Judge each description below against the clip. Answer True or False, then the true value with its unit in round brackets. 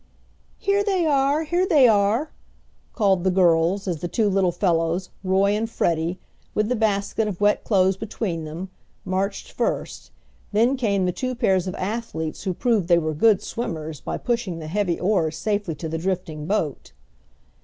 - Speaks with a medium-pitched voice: False (195 Hz)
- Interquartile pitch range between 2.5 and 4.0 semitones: False (4.5 semitones)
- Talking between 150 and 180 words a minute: True (170 wpm)